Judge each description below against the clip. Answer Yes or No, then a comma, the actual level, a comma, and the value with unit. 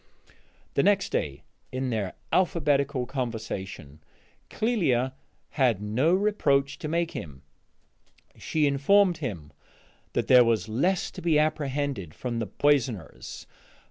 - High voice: No, low, 135 Hz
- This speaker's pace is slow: Yes, slow, 115 wpm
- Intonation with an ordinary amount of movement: No, wide, 5.9 semitones